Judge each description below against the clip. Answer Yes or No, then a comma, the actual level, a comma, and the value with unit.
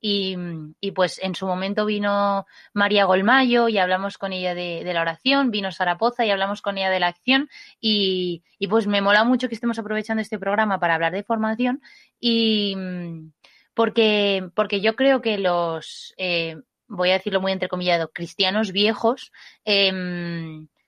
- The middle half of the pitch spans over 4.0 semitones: No, average, 3.3 semitones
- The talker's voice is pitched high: Yes, high, 200 Hz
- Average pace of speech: Yes, average, 165 wpm